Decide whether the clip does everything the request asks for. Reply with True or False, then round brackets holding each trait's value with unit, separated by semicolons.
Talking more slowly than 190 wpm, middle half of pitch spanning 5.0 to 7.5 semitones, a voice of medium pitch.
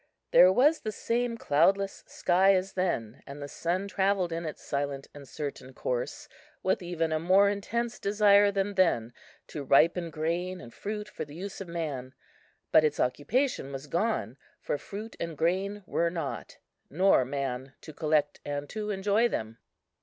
True (165 wpm; 5.6 semitones; 170 Hz)